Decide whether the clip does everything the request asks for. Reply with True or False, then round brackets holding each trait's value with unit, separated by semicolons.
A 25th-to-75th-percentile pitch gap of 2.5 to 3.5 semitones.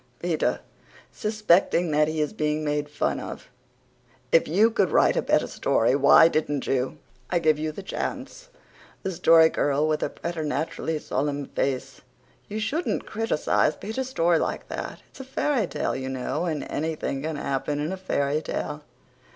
False (4.3 semitones)